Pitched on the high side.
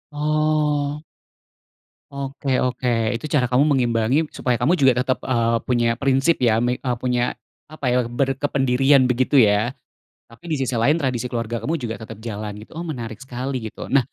No: low, 130 Hz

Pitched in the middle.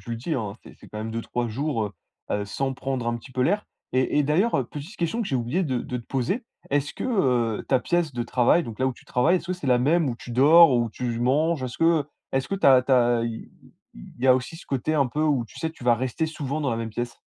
No: low, 130 Hz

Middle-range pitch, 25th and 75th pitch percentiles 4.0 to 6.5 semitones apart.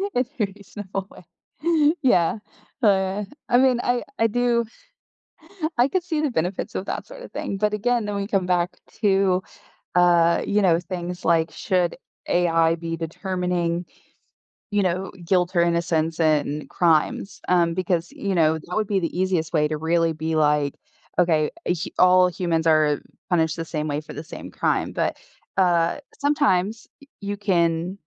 No: medium, 180 Hz; average, 3.3 semitones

